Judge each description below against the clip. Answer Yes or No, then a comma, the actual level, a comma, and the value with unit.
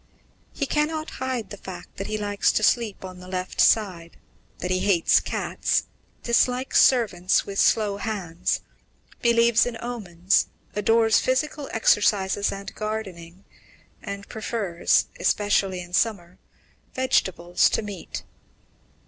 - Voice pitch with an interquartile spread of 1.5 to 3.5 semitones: No, average, 3.9 semitones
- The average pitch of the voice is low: No, high, 205 Hz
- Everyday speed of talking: No, slow, 125 wpm